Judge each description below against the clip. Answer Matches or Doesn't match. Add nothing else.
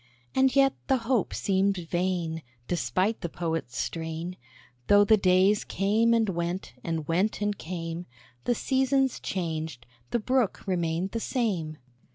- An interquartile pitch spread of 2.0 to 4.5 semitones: Doesn't match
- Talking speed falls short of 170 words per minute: Matches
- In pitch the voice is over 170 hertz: Matches